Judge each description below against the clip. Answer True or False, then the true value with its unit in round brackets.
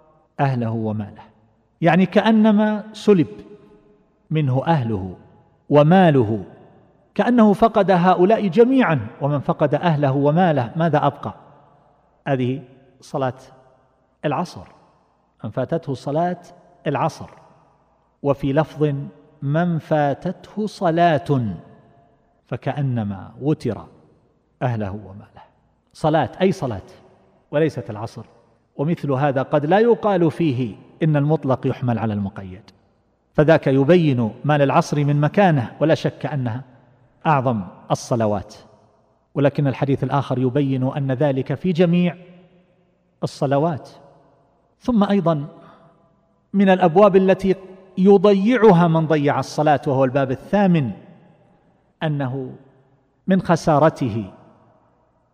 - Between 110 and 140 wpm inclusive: False (90 wpm)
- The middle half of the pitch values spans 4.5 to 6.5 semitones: True (4.8 semitones)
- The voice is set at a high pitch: False (145 Hz)